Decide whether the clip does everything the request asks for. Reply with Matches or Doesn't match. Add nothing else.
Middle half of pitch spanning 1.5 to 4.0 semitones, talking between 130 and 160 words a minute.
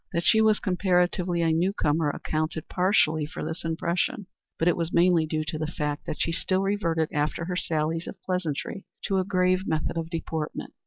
Doesn't match